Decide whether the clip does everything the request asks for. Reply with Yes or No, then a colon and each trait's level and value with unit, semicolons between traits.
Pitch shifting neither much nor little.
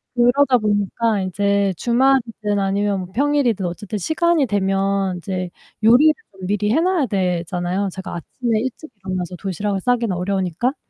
Yes: average, 4.2 semitones